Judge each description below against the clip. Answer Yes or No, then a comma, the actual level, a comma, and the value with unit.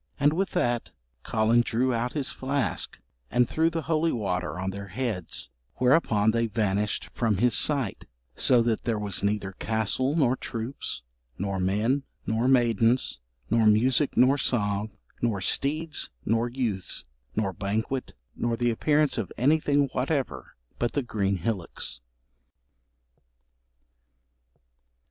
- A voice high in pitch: No, low, 115 Hz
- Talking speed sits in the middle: No, slow, 130 wpm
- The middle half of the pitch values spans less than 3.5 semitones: No, average, 4.1 semitones